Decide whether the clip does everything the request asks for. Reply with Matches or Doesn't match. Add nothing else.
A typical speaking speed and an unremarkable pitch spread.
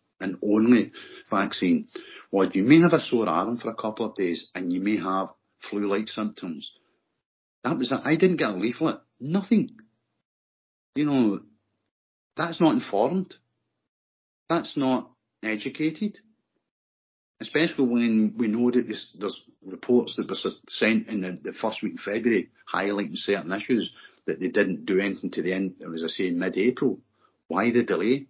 Doesn't match